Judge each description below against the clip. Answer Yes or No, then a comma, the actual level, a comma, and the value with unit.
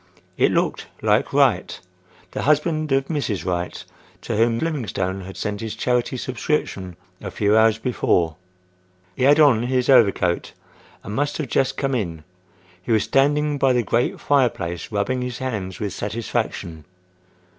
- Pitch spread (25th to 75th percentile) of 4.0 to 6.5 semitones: Yes, average, 5.3 semitones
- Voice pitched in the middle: No, low, 120 Hz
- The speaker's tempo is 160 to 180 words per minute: No, average, 150 wpm